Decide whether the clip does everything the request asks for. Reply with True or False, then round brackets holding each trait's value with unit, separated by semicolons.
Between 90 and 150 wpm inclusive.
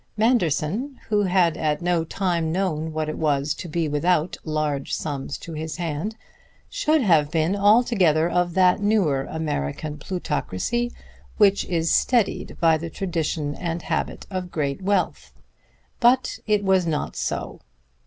True (145 wpm)